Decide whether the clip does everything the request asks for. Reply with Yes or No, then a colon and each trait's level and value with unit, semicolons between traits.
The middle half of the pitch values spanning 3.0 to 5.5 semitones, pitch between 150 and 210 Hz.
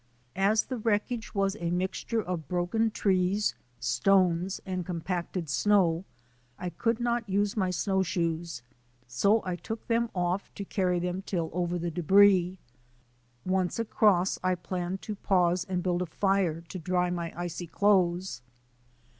No: narrow, 2.4 semitones; medium, 185 Hz